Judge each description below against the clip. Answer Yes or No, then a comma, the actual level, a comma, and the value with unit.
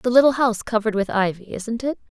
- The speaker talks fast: Yes, fast, 220 wpm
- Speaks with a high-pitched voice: Yes, high, 225 Hz